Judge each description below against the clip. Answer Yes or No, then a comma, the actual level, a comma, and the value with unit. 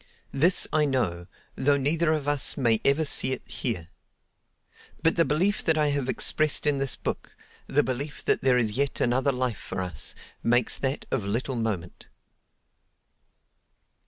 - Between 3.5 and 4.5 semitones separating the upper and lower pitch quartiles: Yes, average, 3.8 semitones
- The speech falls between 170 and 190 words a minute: No, average, 150 wpm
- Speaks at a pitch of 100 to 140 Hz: Yes, low, 135 Hz